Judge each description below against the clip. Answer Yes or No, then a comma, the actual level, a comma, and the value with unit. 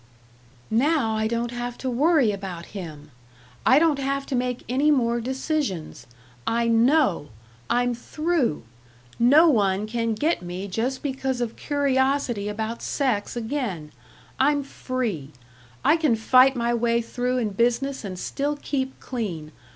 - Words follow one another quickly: No, average, 140 wpm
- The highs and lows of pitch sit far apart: No, average, 4.0 semitones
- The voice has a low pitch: No, high, 245 Hz